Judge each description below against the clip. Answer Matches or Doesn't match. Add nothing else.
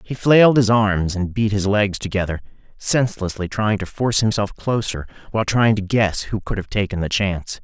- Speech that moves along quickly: Doesn't match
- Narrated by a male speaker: Matches